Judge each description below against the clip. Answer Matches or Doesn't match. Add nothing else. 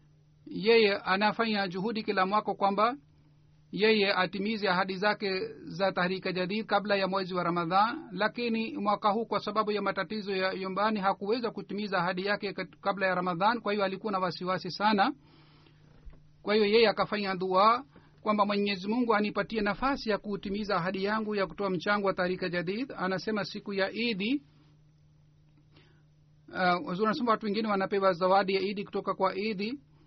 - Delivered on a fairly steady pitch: Matches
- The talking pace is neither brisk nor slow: Matches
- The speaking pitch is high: Matches